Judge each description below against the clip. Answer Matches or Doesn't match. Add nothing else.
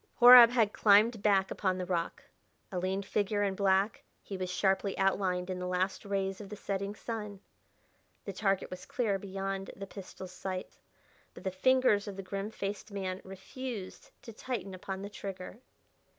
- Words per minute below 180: Matches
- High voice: Matches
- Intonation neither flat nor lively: Doesn't match